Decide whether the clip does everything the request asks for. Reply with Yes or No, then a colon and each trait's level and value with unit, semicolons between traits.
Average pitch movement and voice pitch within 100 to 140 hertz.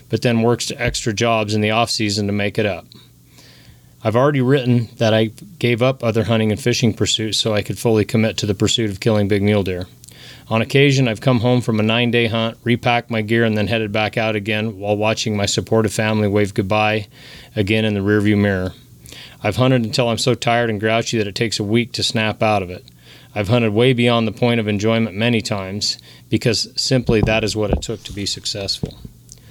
No: narrow, 2.1 semitones; low, 110 Hz